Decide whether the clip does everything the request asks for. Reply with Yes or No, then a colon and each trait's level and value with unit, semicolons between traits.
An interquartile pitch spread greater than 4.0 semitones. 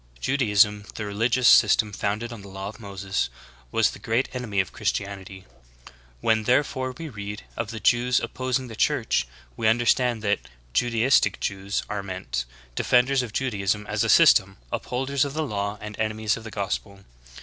No: average, 3.6 semitones